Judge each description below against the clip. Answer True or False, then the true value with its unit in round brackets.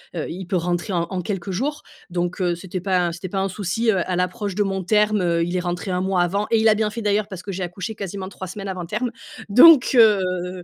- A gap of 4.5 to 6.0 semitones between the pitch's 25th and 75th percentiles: False (2.7 semitones)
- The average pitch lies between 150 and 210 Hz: True (190 Hz)